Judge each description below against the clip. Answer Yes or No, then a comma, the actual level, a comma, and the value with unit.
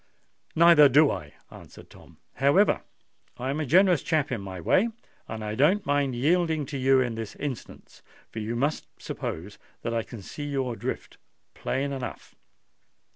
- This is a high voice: No, low, 135 Hz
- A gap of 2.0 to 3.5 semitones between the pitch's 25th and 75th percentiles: No, average, 4.7 semitones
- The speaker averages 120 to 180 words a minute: Yes, average, 165 wpm